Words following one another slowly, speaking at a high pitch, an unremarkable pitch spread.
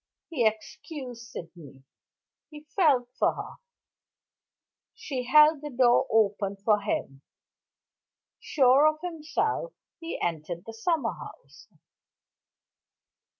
No: slow, 100 wpm; very high, 250 Hz; wide, 6.9 semitones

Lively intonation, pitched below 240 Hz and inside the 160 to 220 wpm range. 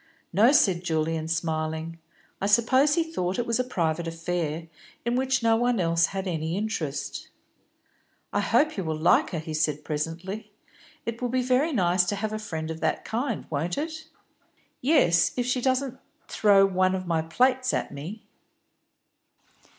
Yes: wide, 7.1 semitones; high, 190 Hz; average, 170 wpm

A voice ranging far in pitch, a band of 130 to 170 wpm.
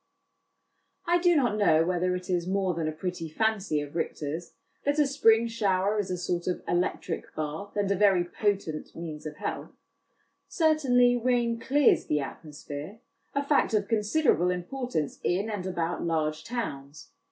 Yes: wide, 5.9 semitones; average, 165 wpm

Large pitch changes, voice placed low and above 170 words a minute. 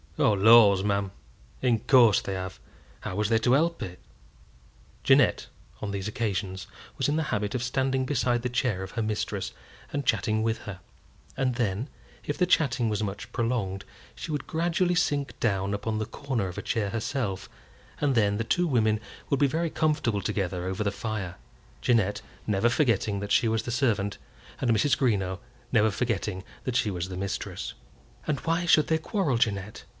No: average, 4.7 semitones; low, 110 Hz; average, 180 wpm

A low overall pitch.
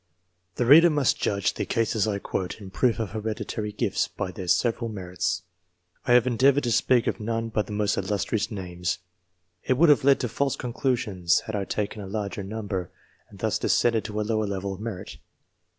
Yes: low, 110 Hz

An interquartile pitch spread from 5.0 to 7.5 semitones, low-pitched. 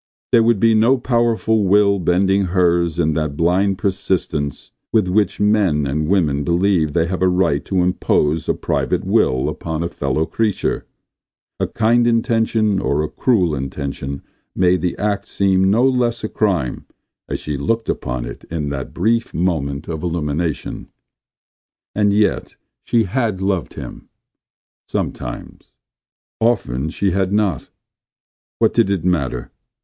Yes: average, 5.3 semitones; very low, 90 Hz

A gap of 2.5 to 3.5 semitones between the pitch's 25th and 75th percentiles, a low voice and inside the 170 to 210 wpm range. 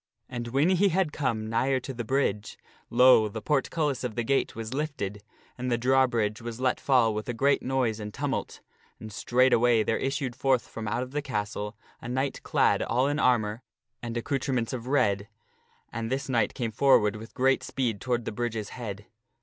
Yes: average, 3.2 semitones; low, 120 Hz; average, 190 wpm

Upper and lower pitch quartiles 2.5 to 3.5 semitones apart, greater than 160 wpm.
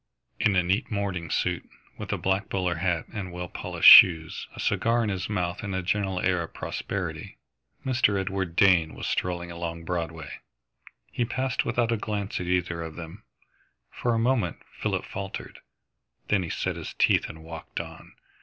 Yes: average, 3.2 semitones; average, 175 wpm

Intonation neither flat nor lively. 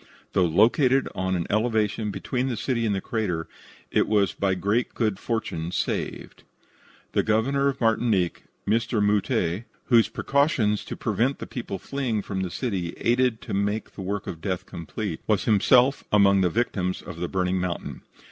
Yes: average, 4.1 semitones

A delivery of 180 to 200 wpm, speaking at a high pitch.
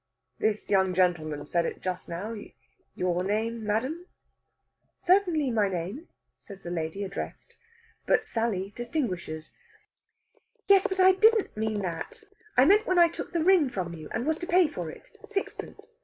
No: average, 155 wpm; high, 220 Hz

